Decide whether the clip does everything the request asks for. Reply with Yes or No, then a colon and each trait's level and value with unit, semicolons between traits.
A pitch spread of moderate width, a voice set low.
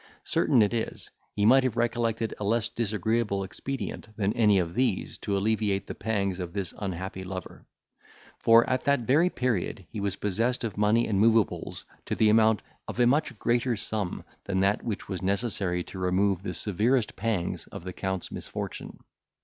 Yes: average, 3.2 semitones; low, 105 Hz